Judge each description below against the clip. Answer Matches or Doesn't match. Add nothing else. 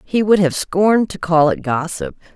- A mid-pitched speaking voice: Matches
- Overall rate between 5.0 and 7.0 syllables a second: Doesn't match